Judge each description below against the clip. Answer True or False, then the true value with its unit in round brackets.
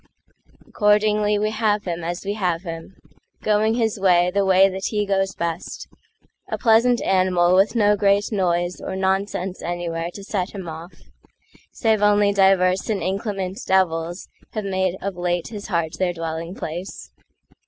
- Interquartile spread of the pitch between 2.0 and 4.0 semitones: True (2.8 semitones)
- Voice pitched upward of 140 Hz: True (190 Hz)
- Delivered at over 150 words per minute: False (140 wpm)